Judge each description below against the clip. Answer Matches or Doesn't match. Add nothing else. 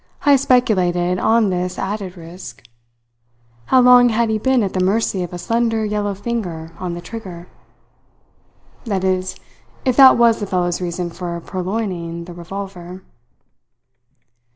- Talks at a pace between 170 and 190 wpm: Doesn't match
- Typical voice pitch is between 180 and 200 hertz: Matches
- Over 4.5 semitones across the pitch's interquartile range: Doesn't match